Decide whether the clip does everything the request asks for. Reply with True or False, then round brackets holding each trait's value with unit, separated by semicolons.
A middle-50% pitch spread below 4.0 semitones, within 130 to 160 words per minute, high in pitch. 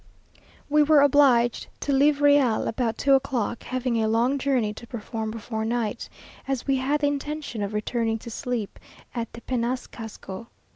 True (3.6 semitones; 155 wpm; 245 Hz)